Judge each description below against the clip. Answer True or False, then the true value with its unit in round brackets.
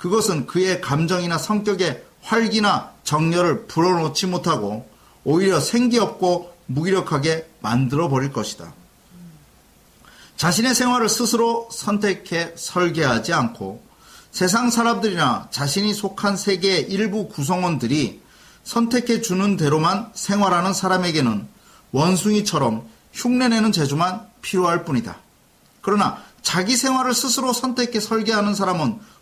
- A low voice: False (185 Hz)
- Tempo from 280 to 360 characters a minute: True (290 characters per minute)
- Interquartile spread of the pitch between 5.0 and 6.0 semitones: True (5.3 semitones)